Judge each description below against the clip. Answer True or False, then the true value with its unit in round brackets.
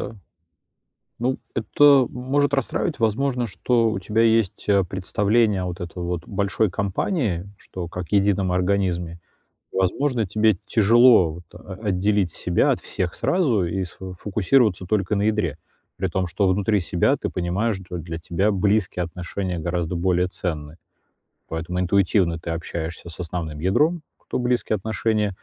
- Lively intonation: False (3.8 semitones)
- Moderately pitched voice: False (95 Hz)